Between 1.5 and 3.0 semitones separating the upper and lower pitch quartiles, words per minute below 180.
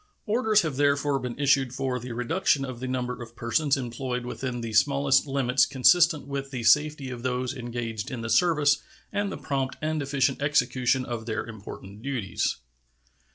Yes: average, 2.7 semitones; average, 170 wpm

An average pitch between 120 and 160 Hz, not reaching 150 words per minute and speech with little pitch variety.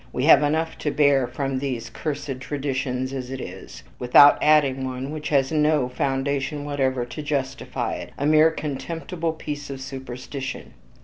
No: medium, 140 Hz; average, 160 wpm; narrow, 2.2 semitones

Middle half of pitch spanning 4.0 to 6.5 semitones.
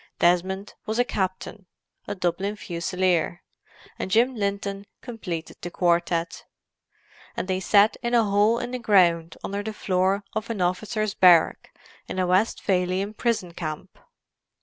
No: average, 3.1 semitones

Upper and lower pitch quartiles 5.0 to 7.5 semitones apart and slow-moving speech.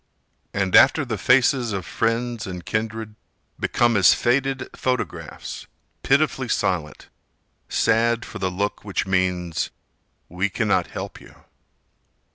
No: average, 4.5 semitones; slow, 115 wpm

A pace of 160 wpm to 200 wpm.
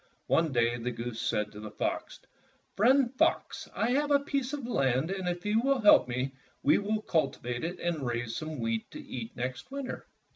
Yes: average, 195 wpm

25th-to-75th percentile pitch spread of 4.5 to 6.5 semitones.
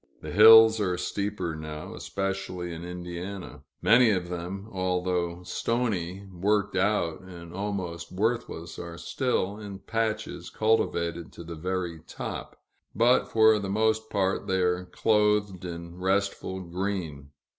No: average, 3.1 semitones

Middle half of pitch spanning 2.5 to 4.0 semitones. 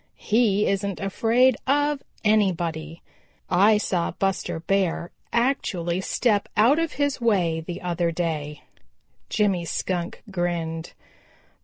No: average, 4.4 semitones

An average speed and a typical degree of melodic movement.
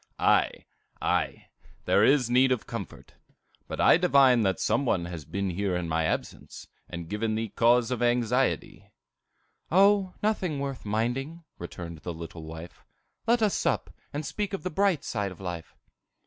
No: average, 160 wpm; wide, 8.4 semitones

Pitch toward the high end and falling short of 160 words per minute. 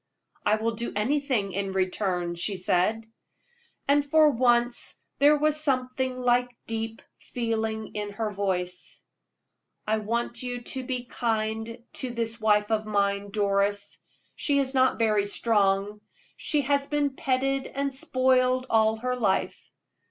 Yes: high, 230 Hz; slow, 135 wpm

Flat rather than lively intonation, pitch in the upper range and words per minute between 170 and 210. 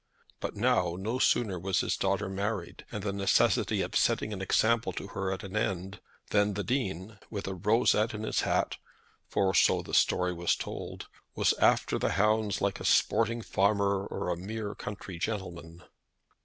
No: narrow, 2.2 semitones; low, 100 Hz; average, 175 wpm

